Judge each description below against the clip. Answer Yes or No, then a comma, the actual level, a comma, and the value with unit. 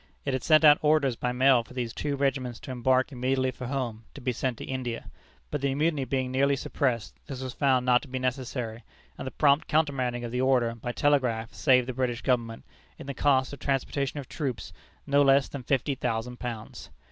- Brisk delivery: Yes, fast, 210 wpm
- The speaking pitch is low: Yes, low, 130 Hz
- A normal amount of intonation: No, narrow, 2.1 semitones